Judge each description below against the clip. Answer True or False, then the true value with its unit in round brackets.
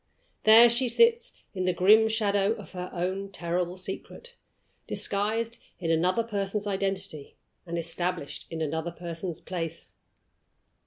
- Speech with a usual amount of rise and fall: True (4.0 semitones)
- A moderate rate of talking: False (125 wpm)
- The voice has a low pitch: False (190 Hz)